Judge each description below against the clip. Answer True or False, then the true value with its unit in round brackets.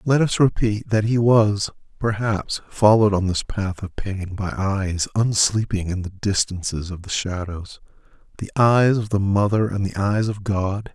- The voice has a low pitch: True (100 Hz)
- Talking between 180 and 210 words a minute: False (170 wpm)